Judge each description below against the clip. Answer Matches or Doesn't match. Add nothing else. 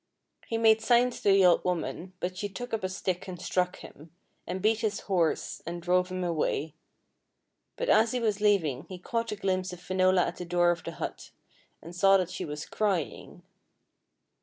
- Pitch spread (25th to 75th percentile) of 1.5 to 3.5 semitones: Matches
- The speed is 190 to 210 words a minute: Matches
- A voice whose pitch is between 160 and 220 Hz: Matches